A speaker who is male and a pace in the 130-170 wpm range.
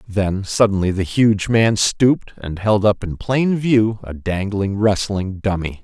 Yes: male; average, 165 wpm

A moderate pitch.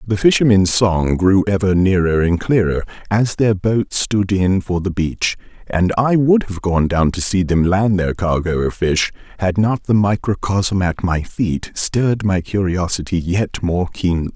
No: very low, 95 Hz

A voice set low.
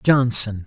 Yes: low, 115 Hz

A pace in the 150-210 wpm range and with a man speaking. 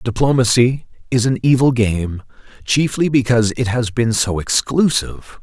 No: slow, 135 wpm; male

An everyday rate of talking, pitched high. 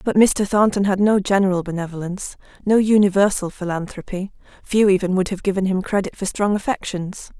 Yes: average, 155 wpm; high, 195 Hz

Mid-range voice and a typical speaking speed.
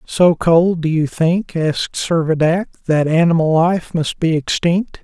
Yes: medium, 165 Hz; average, 155 wpm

